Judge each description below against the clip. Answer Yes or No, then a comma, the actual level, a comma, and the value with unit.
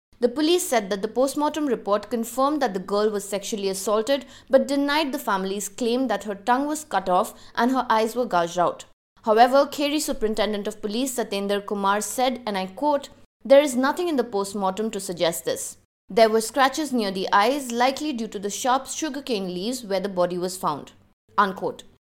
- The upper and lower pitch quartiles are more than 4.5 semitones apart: Yes, average, 5.1 semitones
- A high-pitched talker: Yes, high, 230 Hz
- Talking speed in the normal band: Yes, average, 190 wpm